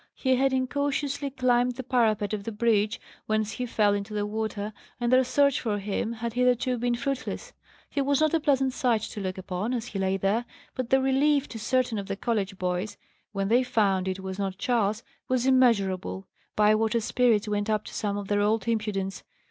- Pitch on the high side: Yes, high, 225 Hz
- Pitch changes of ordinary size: Yes, average, 3.8 semitones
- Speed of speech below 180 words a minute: No, average, 200 wpm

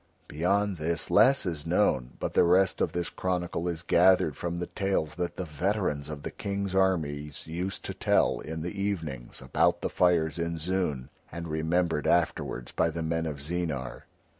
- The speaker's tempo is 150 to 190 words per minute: Yes, average, 175 wpm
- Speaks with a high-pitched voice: No, very low, 85 Hz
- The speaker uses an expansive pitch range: No, average, 2.8 semitones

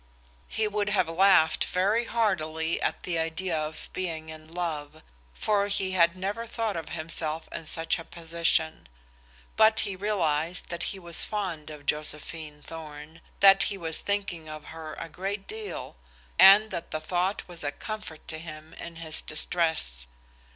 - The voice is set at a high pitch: No, medium, 170 Hz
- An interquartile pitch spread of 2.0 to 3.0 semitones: No, average, 3.7 semitones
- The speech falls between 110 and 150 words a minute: No, average, 160 wpm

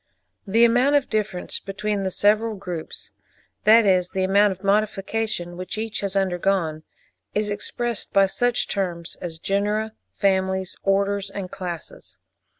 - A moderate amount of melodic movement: No, narrow, 2.3 semitones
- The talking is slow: Yes, slow, 130 wpm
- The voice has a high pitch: Yes, high, 195 Hz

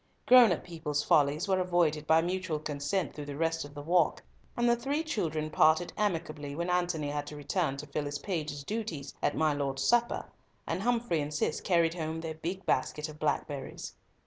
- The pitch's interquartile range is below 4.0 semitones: Yes, average, 3.5 semitones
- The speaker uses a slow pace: No, average, 195 wpm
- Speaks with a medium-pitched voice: Yes, medium, 160 Hz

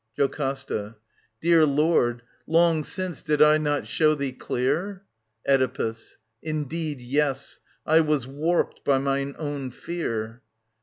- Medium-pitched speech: Yes, medium, 145 Hz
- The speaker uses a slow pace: Yes, slow, 115 wpm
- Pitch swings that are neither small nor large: Yes, average, 3.0 semitones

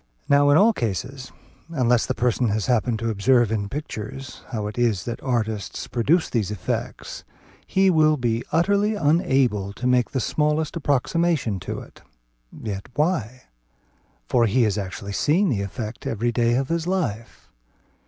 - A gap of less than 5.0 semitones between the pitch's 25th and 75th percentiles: No, wide, 5.5 semitones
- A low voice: Yes, low, 125 Hz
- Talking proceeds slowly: No, average, 155 wpm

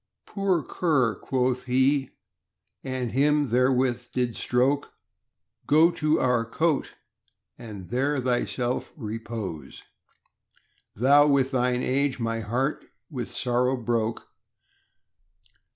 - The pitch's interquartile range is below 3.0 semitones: Yes, narrow, 2.6 semitones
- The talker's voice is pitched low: Yes, low, 125 Hz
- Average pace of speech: No, slow, 100 wpm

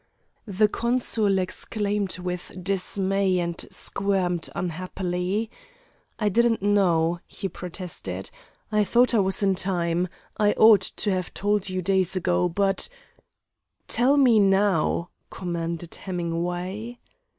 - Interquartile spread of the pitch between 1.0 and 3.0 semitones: Yes, narrow, 2.6 semitones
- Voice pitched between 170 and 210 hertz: Yes, high, 190 Hz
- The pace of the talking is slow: Yes, slow, 115 wpm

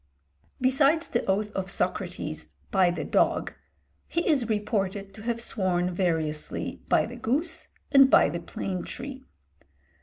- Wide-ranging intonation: Yes, wide, 6.0 semitones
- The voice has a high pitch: Yes, high, 205 Hz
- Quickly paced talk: No, average, 140 wpm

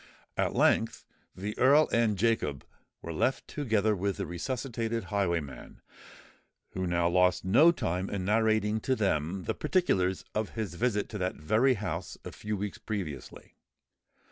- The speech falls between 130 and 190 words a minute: Yes, average, 145 wpm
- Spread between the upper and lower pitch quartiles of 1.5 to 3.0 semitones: No, average, 3.8 semitones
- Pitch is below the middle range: Yes, low, 105 Hz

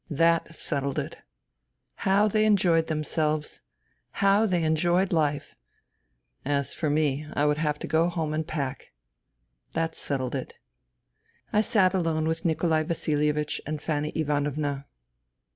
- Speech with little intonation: Yes, narrow, 2.2 semitones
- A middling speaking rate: No, slow, 130 wpm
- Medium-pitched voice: Yes, medium, 155 Hz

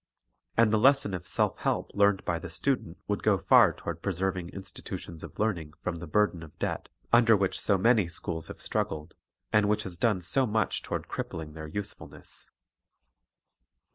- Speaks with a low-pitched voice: Yes, very low, 95 Hz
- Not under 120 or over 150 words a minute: No, average, 170 wpm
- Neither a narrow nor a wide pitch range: Yes, average, 4.0 semitones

